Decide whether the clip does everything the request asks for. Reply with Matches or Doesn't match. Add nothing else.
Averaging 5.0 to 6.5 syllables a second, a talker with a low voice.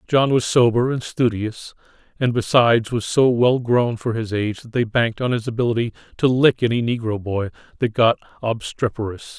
Matches